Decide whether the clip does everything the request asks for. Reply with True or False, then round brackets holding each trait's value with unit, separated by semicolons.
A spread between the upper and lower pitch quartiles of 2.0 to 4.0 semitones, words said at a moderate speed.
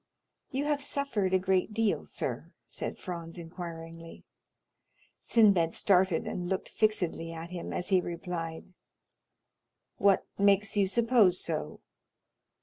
False (3.7 semitones; 120 wpm)